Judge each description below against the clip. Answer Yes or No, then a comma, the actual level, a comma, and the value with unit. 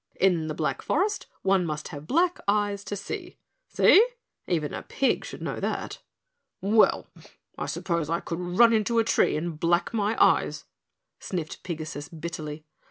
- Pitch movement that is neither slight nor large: Yes, average, 4.9 semitones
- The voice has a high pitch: No, medium, 175 Hz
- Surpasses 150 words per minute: Yes, average, 160 wpm